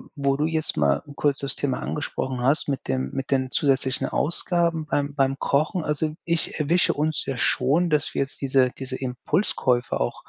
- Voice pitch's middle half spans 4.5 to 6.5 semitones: No, average, 2.8 semitones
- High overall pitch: No, medium, 140 Hz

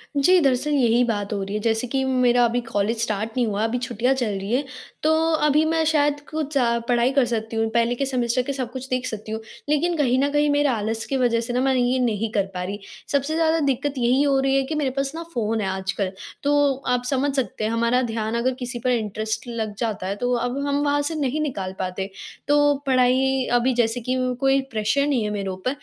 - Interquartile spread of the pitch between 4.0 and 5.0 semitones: No, average, 3.6 semitones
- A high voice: Yes, high, 245 Hz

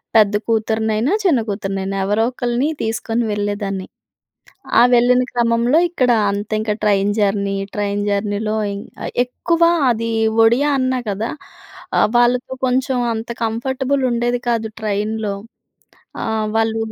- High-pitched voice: Yes, high, 225 Hz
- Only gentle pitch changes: No, average, 3.0 semitones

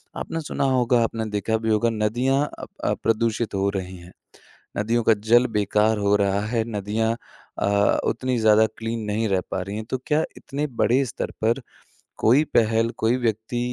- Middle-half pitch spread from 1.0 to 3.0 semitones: Yes, narrow, 2.4 semitones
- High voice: No, low, 110 Hz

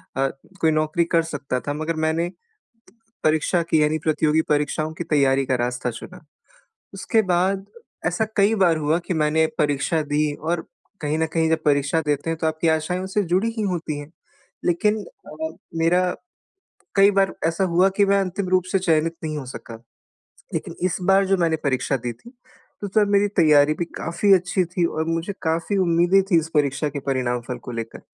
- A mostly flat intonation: No, average, 3.4 semitones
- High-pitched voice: No, medium, 160 Hz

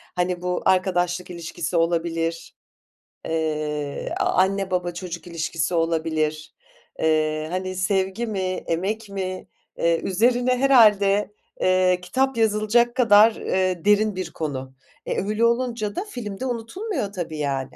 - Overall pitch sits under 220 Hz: Yes, medium, 185 Hz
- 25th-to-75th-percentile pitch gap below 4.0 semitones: No, average, 4.3 semitones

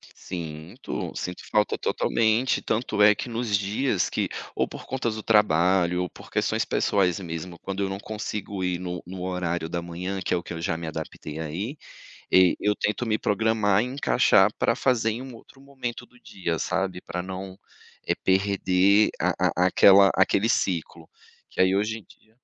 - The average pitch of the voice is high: No, very low, 95 Hz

